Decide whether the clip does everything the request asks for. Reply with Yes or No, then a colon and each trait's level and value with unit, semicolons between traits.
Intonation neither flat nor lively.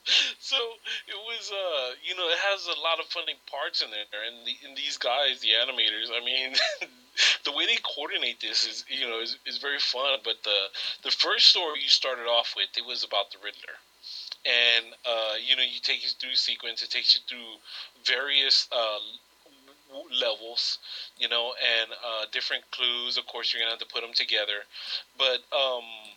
No: wide, 6.0 semitones